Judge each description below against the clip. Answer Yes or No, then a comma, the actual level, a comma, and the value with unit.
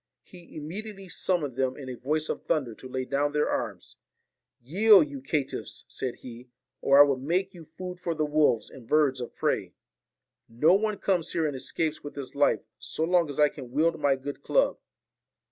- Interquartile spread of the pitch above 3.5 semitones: Yes, average, 4.3 semitones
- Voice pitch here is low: No, medium, 150 Hz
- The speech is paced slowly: No, fast, 205 wpm